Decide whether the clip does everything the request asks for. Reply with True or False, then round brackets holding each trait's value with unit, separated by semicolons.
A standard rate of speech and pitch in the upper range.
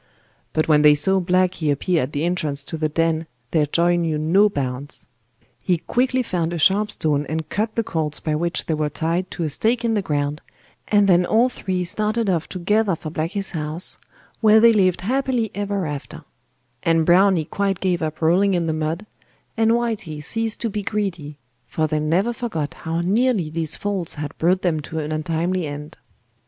False (190 wpm; 170 Hz)